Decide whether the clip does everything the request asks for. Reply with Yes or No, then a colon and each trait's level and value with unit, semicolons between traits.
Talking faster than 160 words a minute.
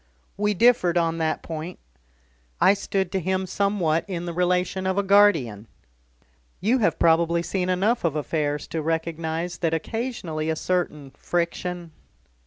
No: average, 145 wpm